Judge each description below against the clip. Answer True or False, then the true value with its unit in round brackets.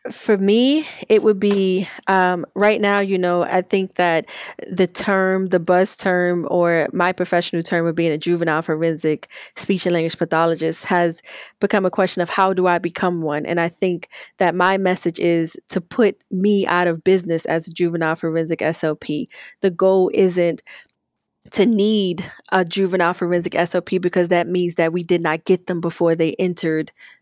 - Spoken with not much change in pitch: True (2.0 semitones)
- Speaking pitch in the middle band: True (180 Hz)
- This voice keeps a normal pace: True (175 wpm)